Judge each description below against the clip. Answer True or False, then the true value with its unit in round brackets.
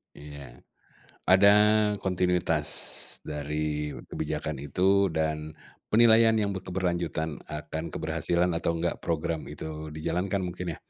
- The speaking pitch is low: True (80 Hz)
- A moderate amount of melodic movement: True (3.1 semitones)